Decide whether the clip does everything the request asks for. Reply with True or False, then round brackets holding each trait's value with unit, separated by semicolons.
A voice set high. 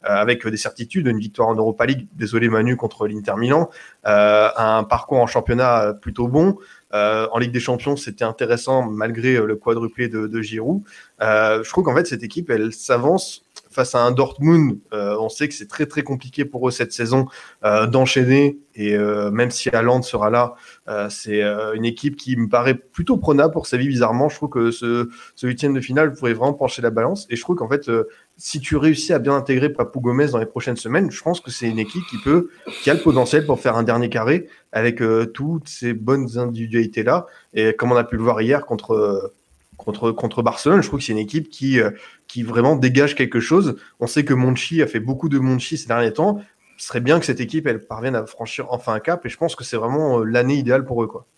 False (125 Hz)